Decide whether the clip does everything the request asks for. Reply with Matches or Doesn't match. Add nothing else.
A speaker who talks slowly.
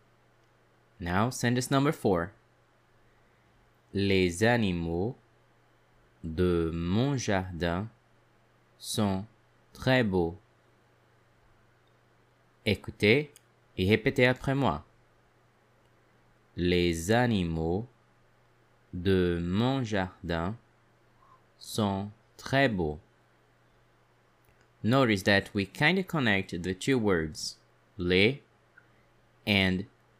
Matches